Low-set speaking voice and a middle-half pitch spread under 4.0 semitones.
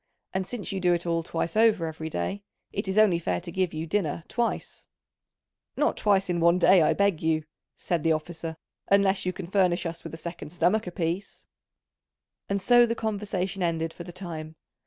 No: medium, 180 Hz; average, 3.1 semitones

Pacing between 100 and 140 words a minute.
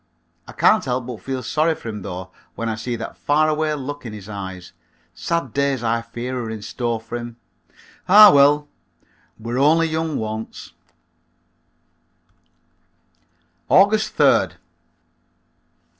Yes: slow, 135 wpm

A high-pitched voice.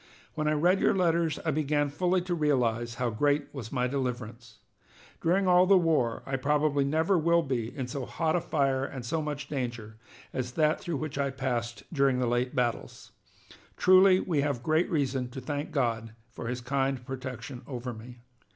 No: medium, 140 Hz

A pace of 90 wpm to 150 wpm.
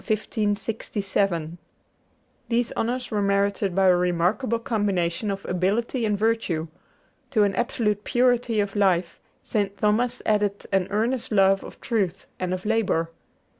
Yes: average, 140 wpm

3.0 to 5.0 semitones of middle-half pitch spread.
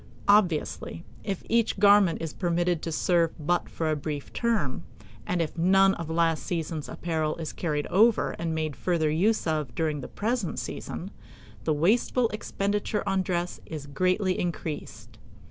Yes: average, 3.6 semitones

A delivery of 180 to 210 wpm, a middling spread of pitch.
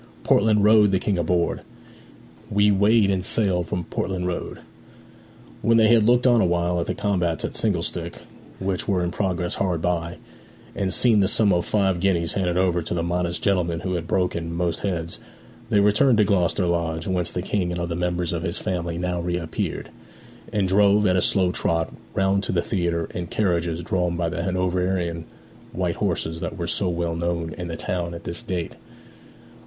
No: average, 190 wpm; narrow, 2.3 semitones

